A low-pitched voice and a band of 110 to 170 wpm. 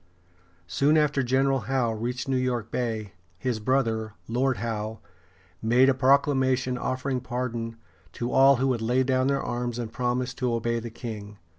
Yes: low, 125 Hz; average, 160 wpm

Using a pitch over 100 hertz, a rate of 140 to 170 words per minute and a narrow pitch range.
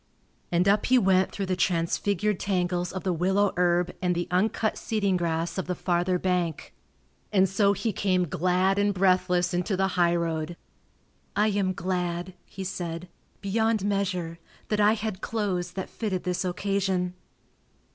Yes: medium, 185 Hz; average, 155 wpm; narrow, 2.1 semitones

